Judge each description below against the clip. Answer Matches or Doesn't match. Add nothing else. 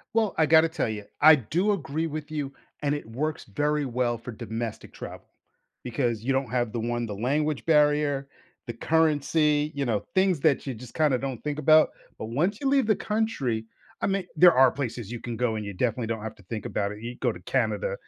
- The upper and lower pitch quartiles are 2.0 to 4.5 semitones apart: Doesn't match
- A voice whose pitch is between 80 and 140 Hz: Matches